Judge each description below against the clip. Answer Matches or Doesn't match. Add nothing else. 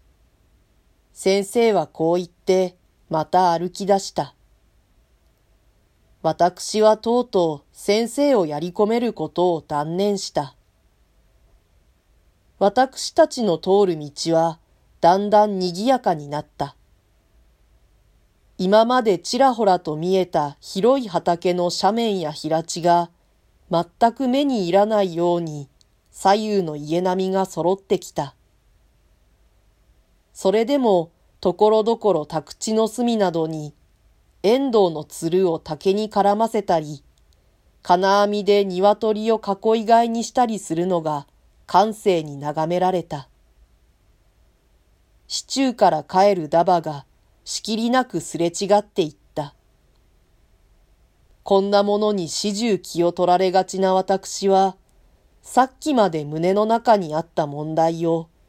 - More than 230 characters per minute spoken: Doesn't match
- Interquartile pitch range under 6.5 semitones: Matches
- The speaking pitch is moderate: Matches